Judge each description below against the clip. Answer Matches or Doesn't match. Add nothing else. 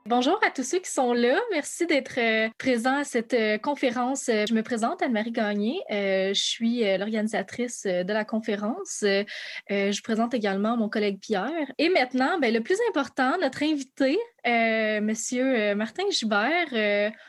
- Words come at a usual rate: Matches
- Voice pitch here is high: Matches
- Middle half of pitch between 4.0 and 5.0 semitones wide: Matches